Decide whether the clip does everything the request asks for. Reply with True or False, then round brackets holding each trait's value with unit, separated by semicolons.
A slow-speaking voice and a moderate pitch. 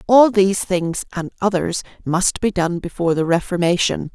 True (130 wpm; 180 Hz)